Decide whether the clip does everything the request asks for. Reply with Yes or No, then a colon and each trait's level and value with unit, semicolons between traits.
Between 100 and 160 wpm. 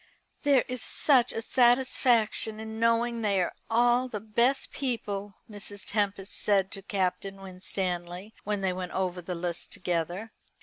Yes: average, 145 wpm